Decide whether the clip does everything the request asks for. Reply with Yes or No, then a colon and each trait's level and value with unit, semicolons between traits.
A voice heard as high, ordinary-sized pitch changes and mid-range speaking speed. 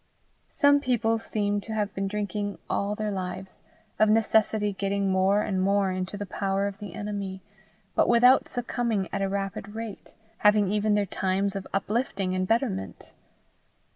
No: high, 205 Hz; narrow, 1.8 semitones; average, 160 wpm